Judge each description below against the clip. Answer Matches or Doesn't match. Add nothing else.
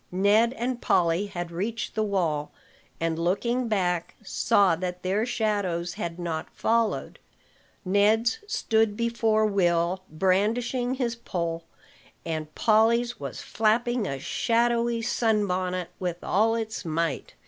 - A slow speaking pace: Matches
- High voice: Matches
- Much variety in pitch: Doesn't match